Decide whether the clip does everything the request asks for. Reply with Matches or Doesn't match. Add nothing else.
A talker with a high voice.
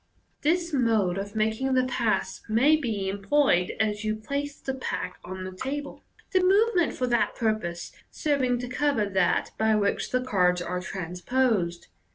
Matches